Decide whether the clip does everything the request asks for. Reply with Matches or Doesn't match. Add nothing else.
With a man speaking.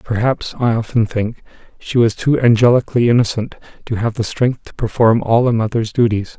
Matches